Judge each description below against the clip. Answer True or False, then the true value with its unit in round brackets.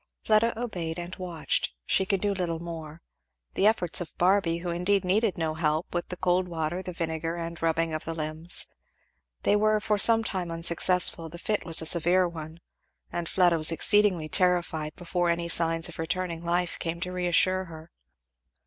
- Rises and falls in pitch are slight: True (2.1 semitones)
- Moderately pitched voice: True (175 Hz)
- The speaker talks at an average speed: True (175 wpm)